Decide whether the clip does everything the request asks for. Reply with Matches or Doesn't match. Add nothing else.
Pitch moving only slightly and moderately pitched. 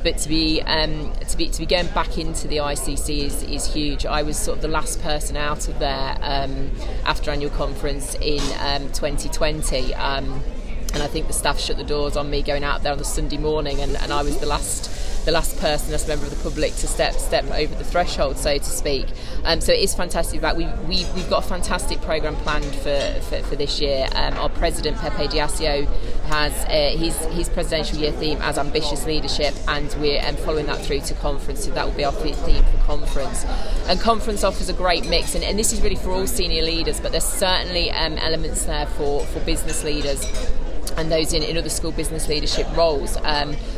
Matches